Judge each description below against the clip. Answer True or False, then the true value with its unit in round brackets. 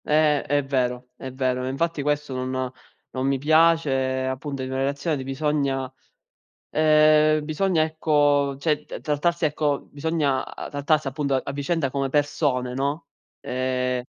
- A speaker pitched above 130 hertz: True (140 Hz)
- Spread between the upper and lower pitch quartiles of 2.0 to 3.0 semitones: True (2.6 semitones)